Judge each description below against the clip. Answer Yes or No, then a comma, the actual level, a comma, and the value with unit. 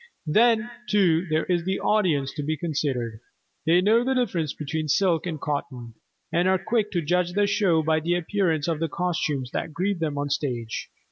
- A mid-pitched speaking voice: Yes, medium, 165 Hz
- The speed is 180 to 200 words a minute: Yes, average, 195 wpm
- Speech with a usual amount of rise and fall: Yes, average, 4.3 semitones